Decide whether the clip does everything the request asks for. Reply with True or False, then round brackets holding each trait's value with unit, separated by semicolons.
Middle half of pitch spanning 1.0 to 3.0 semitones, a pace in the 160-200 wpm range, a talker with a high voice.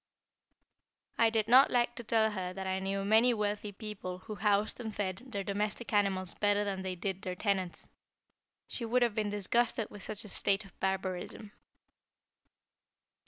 True (2.4 semitones; 165 wpm; 205 Hz)